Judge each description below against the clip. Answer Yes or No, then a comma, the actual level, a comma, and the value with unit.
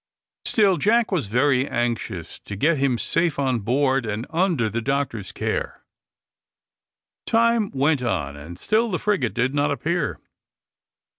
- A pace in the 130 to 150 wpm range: Yes, average, 140 wpm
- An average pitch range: No, wide, 6.6 semitones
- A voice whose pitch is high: No, low, 135 Hz